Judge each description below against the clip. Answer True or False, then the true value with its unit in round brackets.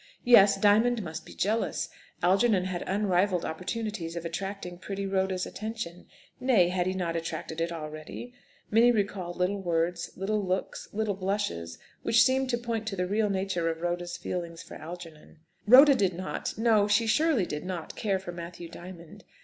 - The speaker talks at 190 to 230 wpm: False (165 wpm)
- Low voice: False (190 Hz)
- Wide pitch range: False (3.6 semitones)